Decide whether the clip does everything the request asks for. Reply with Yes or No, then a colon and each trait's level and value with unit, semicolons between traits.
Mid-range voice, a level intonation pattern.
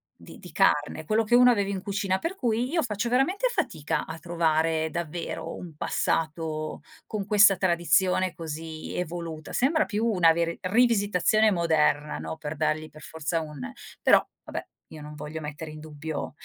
No: medium, 170 Hz; average, 5.0 semitones